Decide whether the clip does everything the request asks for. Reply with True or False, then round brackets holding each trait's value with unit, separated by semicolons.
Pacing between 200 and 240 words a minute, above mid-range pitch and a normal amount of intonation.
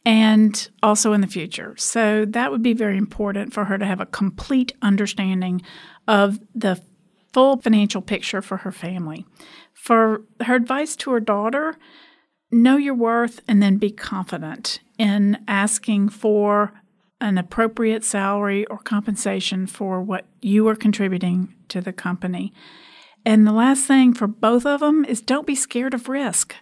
False (155 wpm; 215 Hz; 3.3 semitones)